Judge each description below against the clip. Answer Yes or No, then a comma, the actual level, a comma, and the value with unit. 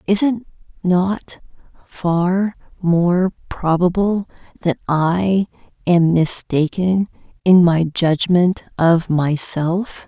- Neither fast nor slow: No, slow, 90 wpm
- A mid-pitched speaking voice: Yes, medium, 180 Hz